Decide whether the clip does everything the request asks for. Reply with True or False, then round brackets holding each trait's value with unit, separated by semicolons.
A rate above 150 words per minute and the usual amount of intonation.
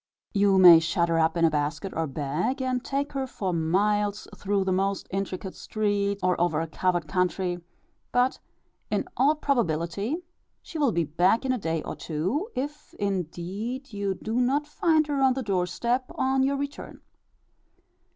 False (170 wpm; 6.9 semitones)